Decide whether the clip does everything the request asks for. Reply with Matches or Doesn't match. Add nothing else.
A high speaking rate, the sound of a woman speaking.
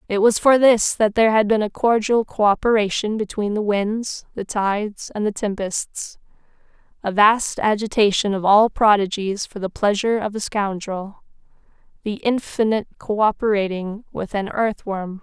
Doesn't match